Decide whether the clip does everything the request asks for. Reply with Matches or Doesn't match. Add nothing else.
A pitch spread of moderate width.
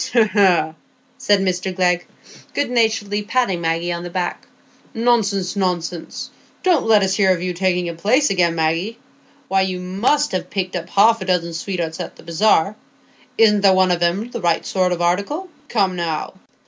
Matches